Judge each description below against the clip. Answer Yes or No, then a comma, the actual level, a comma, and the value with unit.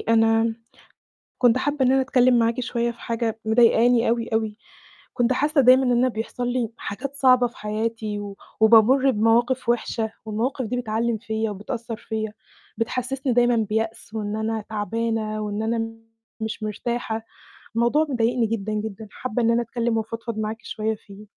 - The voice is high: Yes, high, 230 Hz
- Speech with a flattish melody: Yes, narrow, 1.9 semitones